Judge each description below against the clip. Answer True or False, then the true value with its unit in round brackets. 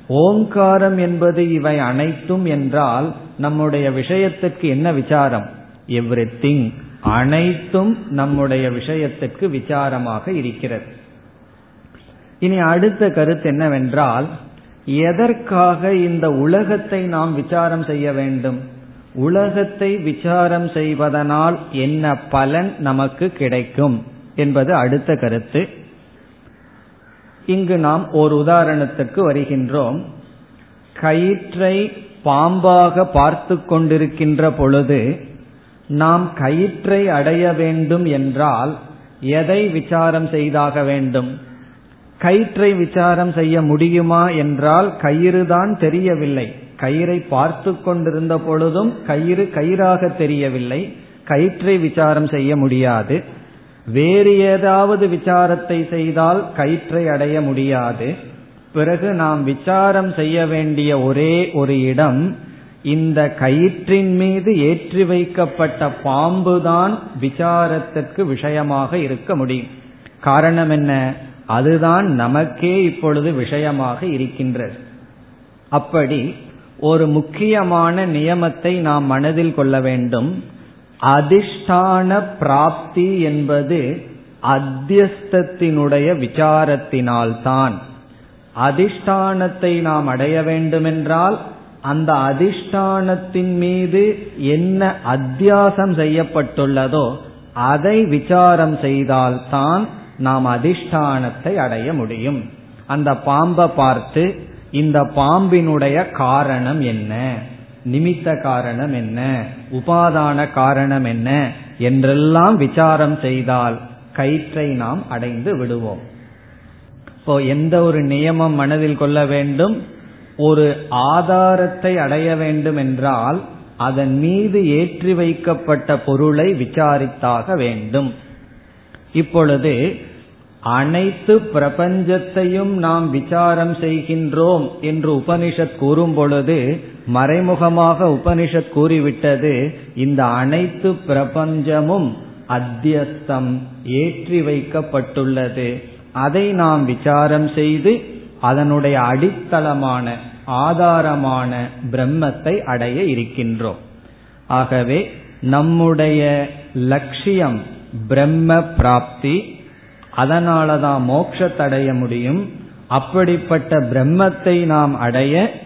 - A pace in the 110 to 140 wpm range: False (75 wpm)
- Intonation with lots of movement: False (4.4 semitones)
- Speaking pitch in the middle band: True (150 Hz)